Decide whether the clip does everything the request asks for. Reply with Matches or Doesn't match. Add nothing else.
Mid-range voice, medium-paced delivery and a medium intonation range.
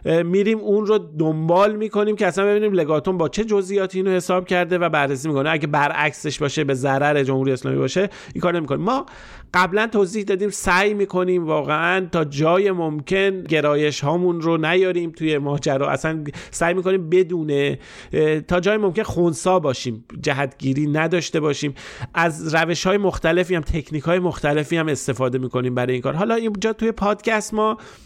Doesn't match